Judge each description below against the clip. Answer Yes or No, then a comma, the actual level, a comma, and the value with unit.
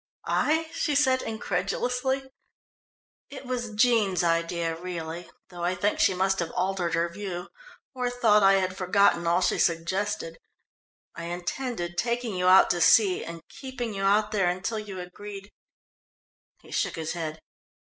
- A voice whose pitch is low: No, high, 190 Hz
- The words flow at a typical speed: Yes, average, 155 wpm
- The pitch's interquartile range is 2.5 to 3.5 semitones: No, average, 4.6 semitones